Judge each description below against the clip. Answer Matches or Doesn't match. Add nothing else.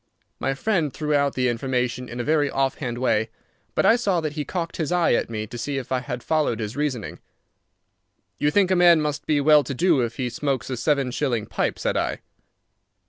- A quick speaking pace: Matches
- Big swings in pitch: Doesn't match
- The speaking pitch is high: Doesn't match